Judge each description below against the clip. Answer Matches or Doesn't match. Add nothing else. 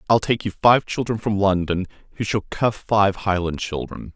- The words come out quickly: Doesn't match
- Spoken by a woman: Doesn't match